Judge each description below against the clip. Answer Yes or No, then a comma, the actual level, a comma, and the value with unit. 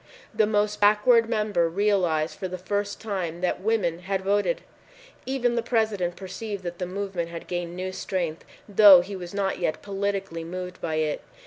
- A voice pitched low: No, high, 190 Hz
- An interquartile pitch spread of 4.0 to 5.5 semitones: No, average, 2.9 semitones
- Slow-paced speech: No, average, 175 wpm